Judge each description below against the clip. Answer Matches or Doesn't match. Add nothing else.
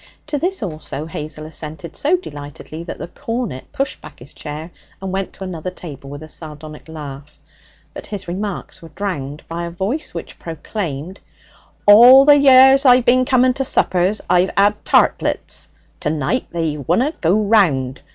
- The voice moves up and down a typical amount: Doesn't match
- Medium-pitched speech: Matches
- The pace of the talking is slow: Doesn't match